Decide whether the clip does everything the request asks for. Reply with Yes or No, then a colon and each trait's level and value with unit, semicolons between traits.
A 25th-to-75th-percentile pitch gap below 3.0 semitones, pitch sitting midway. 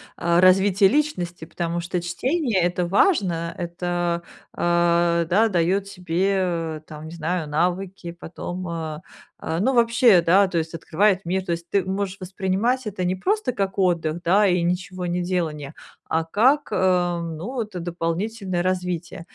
Yes: narrow, 2.4 semitones; medium, 180 Hz